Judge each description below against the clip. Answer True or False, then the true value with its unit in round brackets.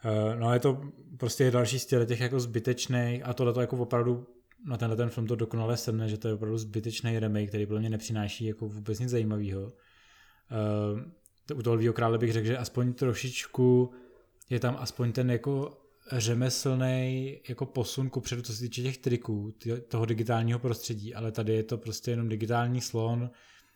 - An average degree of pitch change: False (1.8 semitones)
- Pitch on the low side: True (120 Hz)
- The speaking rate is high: True (180 wpm)